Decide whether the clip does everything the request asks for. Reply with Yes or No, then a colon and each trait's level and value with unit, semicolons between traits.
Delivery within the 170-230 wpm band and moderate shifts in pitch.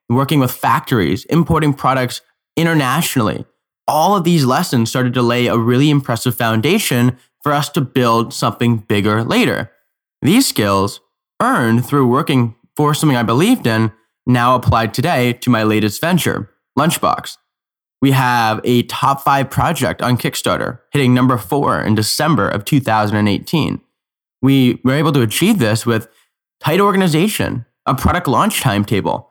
No: average, 145 wpm; average, 4.2 semitones